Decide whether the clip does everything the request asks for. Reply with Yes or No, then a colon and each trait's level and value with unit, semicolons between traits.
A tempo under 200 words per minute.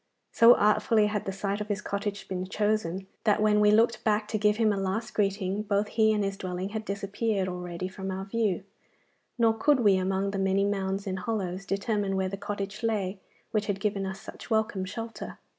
No: fast, 205 wpm